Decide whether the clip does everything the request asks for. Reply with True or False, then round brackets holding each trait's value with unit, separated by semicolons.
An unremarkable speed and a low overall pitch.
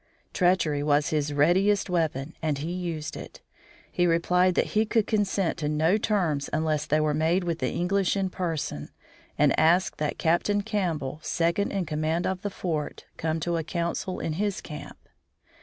False (175 wpm; 170 Hz)